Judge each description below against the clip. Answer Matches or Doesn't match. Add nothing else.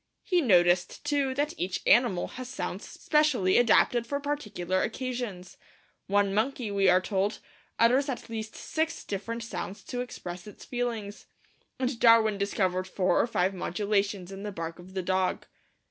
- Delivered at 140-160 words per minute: Matches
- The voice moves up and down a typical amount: Matches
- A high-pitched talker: Matches